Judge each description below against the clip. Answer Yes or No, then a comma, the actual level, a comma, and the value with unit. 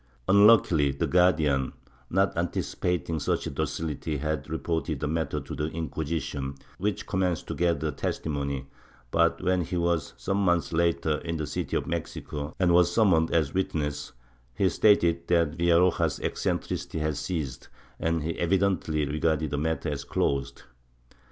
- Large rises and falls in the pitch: No, average, 2.7 semitones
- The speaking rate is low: No, average, 145 wpm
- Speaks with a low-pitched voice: Yes, very low, 80 Hz